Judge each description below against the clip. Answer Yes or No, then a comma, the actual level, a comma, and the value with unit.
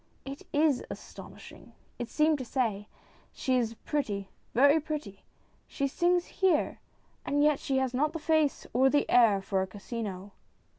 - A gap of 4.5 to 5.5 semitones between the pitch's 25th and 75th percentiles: Yes, average, 5.2 semitones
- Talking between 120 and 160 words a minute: No, average, 170 wpm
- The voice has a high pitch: Yes, very high, 265 Hz